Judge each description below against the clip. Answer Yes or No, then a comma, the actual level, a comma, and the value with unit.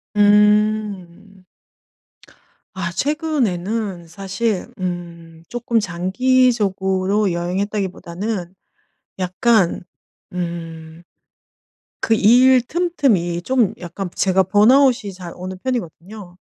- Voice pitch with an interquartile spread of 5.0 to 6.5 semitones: No, average, 4.3 semitones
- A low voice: No, high, 195 Hz